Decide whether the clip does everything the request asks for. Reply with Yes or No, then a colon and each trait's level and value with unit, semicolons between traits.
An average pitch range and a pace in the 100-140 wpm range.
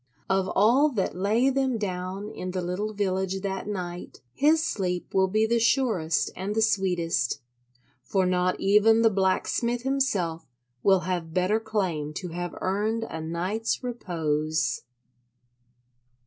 Yes: average, 3.7 semitones; slow, 135 wpm